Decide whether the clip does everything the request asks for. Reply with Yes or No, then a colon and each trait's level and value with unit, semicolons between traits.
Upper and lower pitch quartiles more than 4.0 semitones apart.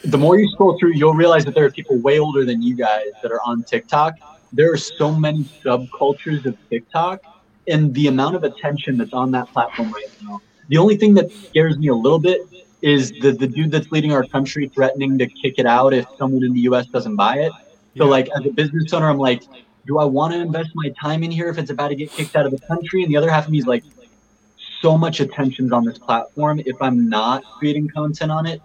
No: average, 3.5 semitones